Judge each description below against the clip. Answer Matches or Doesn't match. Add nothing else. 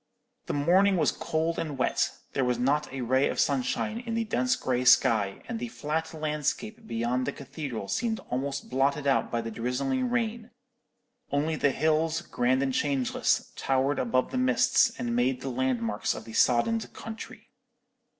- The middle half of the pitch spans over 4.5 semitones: Matches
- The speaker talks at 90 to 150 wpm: Doesn't match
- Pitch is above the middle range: Doesn't match